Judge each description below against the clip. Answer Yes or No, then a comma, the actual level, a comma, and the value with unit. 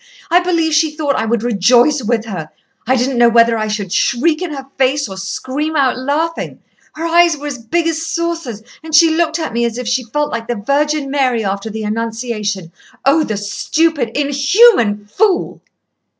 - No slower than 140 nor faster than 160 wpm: No, average, 190 wpm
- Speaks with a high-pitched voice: Yes, very high, 265 Hz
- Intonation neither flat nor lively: No, wide, 5.7 semitones